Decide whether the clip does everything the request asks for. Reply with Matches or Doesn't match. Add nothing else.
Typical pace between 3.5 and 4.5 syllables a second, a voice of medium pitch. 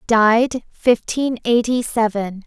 Doesn't match